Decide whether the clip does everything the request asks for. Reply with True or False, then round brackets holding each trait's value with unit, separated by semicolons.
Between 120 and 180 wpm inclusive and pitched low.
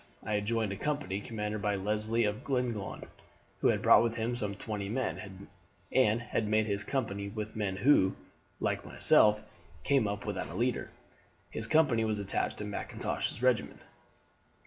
True (170 wpm; 105 Hz)